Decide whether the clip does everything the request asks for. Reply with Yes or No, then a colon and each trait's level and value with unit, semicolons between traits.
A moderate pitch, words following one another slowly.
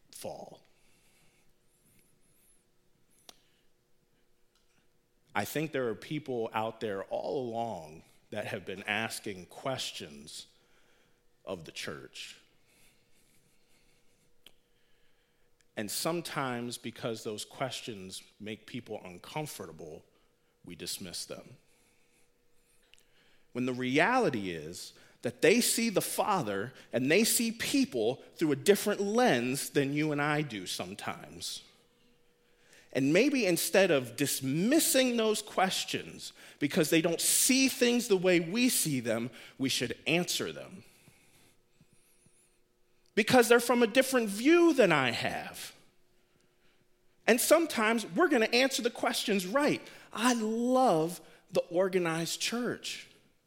Yes: medium, 170 Hz; slow, 105 wpm